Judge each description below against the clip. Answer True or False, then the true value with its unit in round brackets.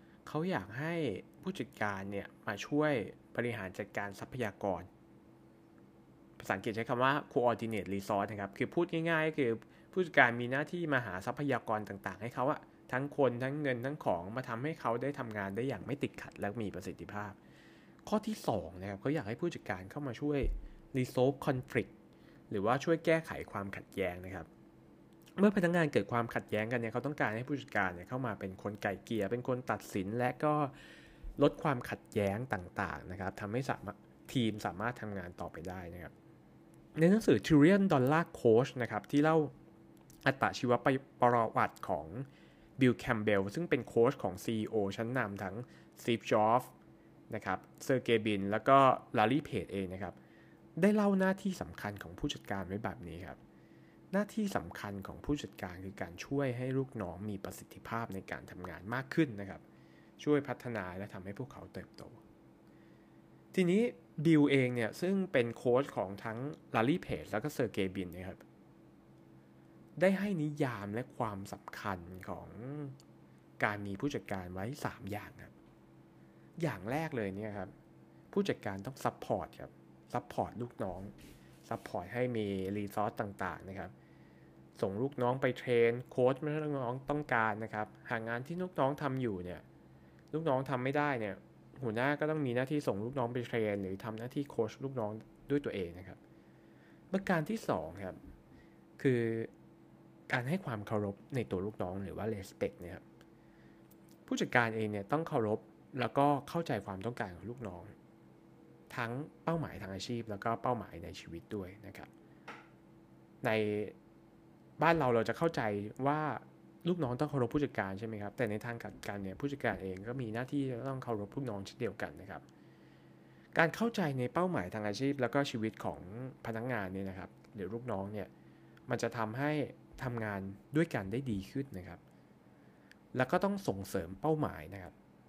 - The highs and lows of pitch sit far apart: True (6.1 semitones)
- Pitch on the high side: False (110 Hz)